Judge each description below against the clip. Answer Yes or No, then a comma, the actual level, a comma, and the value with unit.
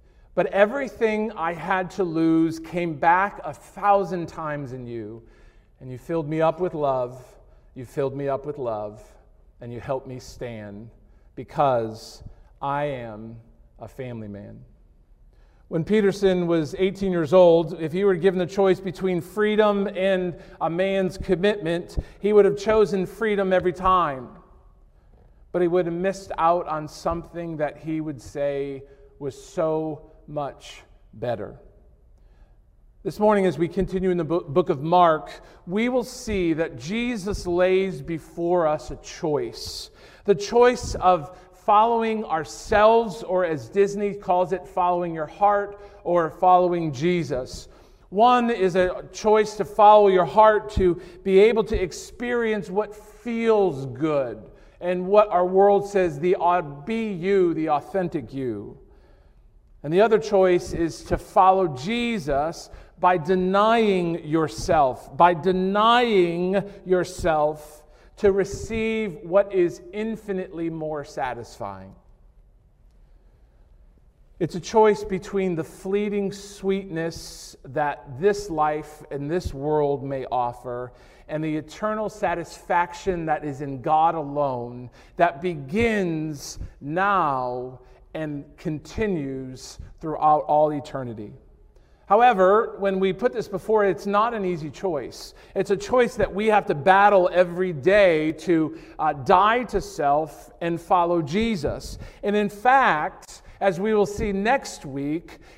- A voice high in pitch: No, medium, 180 Hz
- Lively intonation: No, average, 4.9 semitones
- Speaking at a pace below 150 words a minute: Yes, slow, 135 wpm